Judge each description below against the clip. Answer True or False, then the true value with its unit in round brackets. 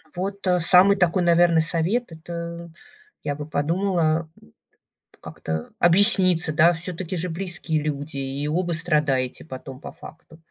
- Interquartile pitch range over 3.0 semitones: False (2.7 semitones)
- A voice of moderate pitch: True (165 Hz)